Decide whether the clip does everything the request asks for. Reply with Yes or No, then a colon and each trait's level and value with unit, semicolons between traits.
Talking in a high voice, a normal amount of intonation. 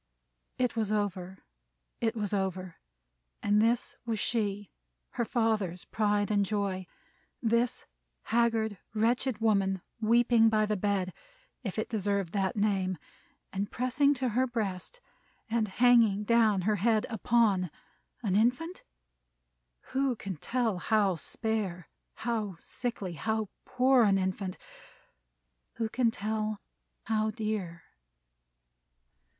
Yes: high, 215 Hz; average, 3.0 semitones